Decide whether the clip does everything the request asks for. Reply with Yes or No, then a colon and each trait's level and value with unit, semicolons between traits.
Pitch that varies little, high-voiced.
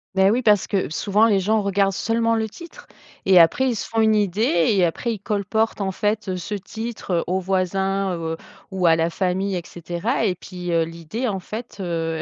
No: average, 3.5 semitones; high, 195 Hz